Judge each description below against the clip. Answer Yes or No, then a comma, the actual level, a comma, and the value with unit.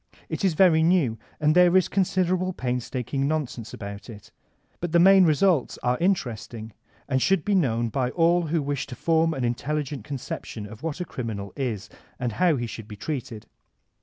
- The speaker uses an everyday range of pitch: No, wide, 6.6 semitones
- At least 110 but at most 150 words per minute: No, average, 180 wpm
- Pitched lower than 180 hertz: Yes, medium, 140 Hz